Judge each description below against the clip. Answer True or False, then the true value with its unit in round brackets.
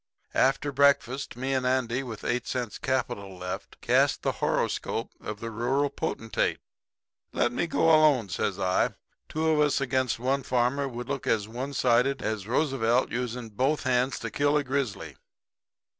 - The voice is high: False (125 Hz)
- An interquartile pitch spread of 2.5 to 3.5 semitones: True (3.0 semitones)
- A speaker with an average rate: True (160 wpm)